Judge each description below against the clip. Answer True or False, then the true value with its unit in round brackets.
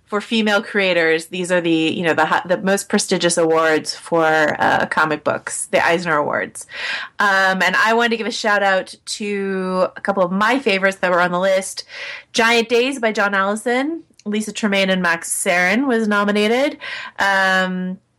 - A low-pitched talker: False (195 Hz)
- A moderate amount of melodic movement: True (3.8 semitones)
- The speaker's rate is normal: True (175 wpm)